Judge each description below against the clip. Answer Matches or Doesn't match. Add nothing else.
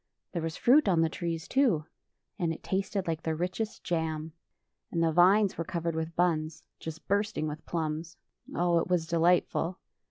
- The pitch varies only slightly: Matches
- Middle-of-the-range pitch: Matches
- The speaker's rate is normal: Matches